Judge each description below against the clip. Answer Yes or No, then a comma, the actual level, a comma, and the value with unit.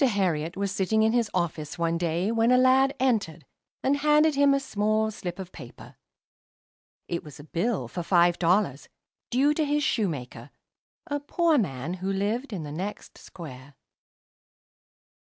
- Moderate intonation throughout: No, wide, 7.1 semitones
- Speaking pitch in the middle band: No, high, 200 Hz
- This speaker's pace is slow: No, average, 155 wpm